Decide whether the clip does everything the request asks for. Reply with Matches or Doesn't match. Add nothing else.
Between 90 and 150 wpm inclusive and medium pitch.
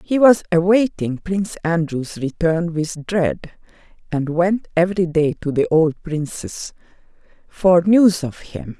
Matches